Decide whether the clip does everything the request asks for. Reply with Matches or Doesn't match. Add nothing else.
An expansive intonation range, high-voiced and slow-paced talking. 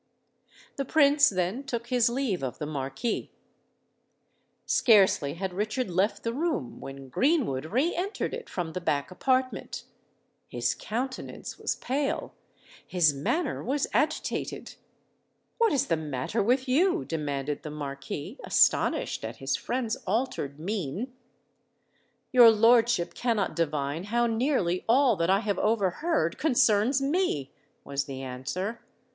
Matches